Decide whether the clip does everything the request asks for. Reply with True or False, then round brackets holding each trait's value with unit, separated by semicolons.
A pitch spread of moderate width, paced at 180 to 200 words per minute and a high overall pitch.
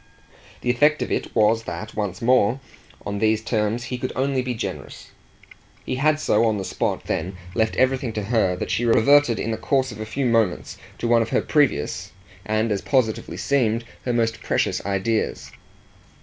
False (3.0 semitones; 185 wpm; 115 Hz)